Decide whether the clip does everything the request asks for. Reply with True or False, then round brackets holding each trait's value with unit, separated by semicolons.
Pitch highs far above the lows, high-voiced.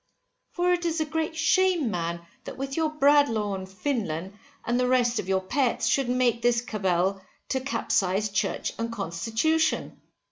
True (6.9 semitones; 240 Hz)